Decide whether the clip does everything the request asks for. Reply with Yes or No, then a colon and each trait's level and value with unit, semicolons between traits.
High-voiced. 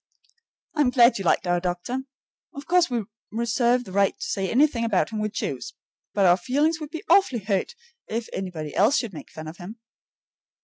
Yes: high, 225 Hz